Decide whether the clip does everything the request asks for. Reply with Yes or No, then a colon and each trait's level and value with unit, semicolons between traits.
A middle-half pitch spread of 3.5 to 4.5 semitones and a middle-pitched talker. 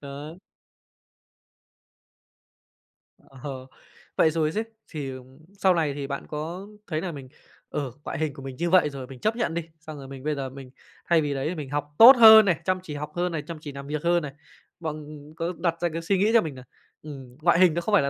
Yes: average, 3.8 semitones; medium, 155 Hz